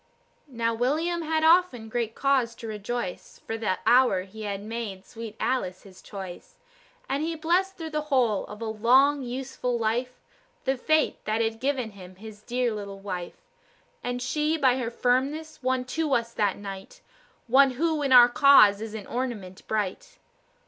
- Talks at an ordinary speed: Yes, average, 170 wpm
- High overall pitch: Yes, high, 240 Hz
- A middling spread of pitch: Yes, average, 4.5 semitones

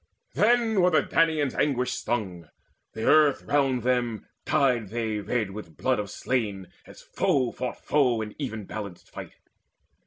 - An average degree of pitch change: Yes, average, 4.9 semitones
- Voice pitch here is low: Yes, low, 125 Hz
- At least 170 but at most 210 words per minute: No, average, 155 wpm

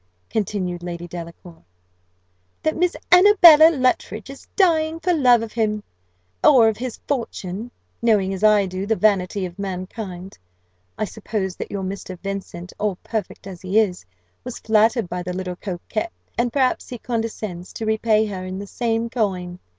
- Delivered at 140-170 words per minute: Yes, average, 160 wpm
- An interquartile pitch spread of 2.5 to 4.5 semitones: Yes, average, 4.2 semitones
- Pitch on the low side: No, high, 210 Hz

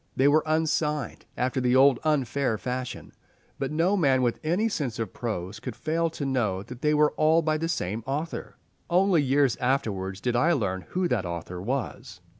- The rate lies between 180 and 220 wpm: Yes, average, 185 wpm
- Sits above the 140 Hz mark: No, low, 135 Hz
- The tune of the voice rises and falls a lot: No, average, 4.8 semitones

